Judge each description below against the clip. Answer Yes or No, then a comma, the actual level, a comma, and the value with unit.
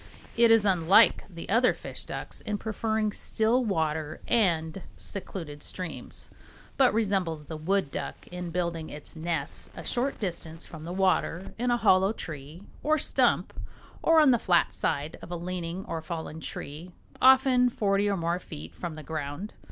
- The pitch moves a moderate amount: Yes, average, 5.0 semitones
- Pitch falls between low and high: Yes, medium, 180 Hz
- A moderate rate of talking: Yes, average, 165 wpm